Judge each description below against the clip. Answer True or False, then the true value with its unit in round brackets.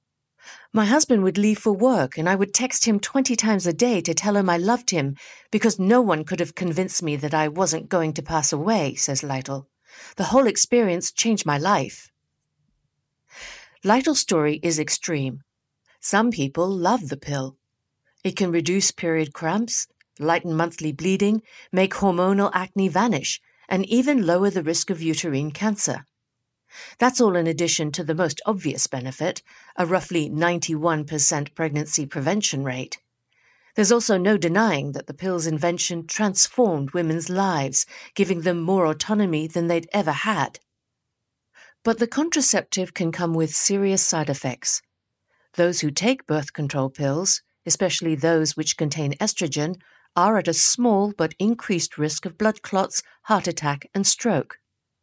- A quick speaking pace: False (155 wpm)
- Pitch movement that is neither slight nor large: True (4.9 semitones)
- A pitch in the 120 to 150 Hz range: False (175 Hz)